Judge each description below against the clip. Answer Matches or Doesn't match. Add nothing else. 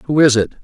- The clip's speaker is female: Doesn't match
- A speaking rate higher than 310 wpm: Doesn't match